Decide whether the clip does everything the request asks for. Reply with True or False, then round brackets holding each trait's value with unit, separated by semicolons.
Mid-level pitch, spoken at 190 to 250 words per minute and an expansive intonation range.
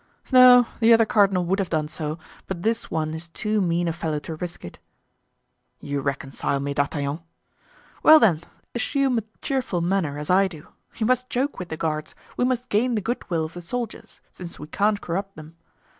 True (180 Hz; 195 wpm; 6.3 semitones)